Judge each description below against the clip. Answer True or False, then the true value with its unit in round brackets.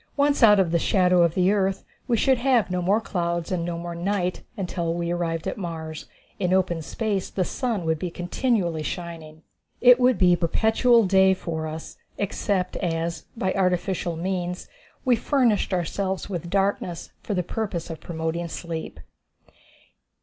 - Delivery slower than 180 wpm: True (165 wpm)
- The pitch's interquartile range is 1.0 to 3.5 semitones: True (3.0 semitones)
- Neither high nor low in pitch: True (180 Hz)